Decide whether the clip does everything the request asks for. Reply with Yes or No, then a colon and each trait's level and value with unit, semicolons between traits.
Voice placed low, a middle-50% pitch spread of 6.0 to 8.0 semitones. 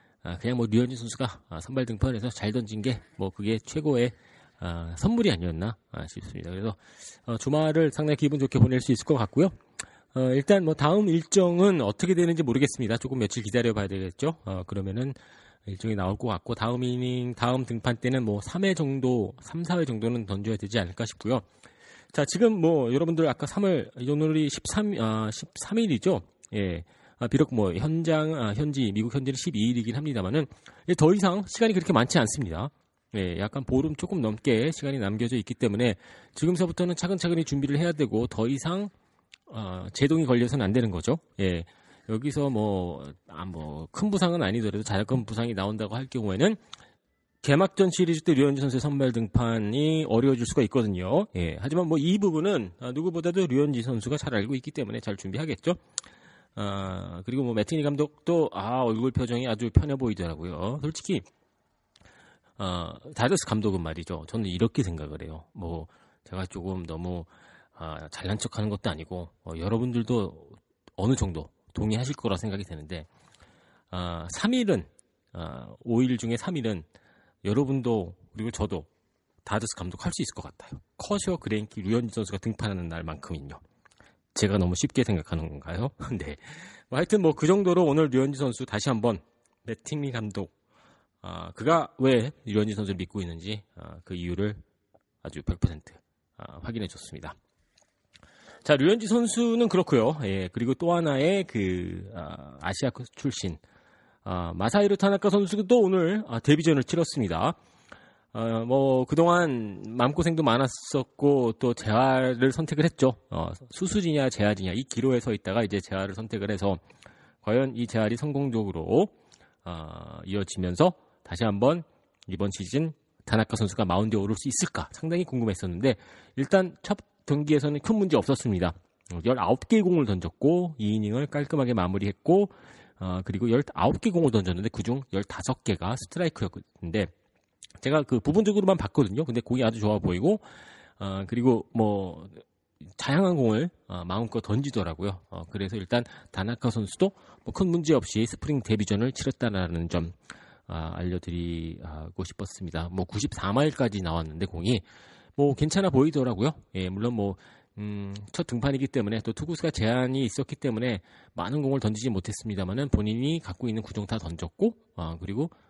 Yes: low, 115 Hz; wide, 6.7 semitones